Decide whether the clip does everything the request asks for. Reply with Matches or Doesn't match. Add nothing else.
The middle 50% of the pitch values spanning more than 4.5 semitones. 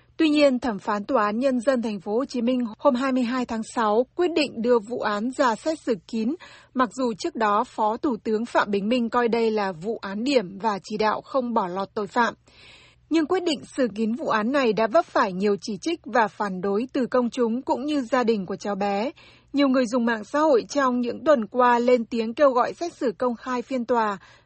Doesn't match